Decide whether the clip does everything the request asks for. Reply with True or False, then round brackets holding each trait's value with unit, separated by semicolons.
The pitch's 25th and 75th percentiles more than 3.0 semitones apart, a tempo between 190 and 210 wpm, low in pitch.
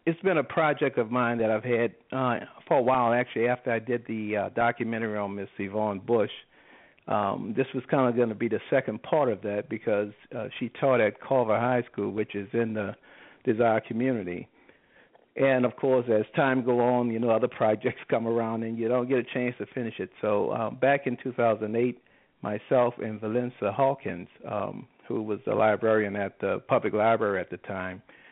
False (2.6 semitones; 200 wpm; 115 Hz)